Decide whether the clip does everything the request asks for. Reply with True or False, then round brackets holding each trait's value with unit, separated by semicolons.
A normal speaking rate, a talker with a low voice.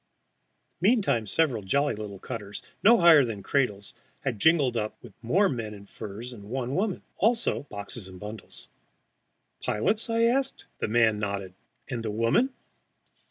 True (150 wpm; 115 Hz)